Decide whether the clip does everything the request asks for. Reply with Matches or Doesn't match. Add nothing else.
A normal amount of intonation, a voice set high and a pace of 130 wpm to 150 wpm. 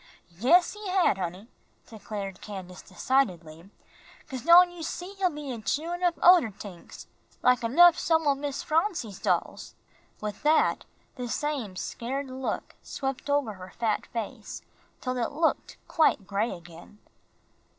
Doesn't match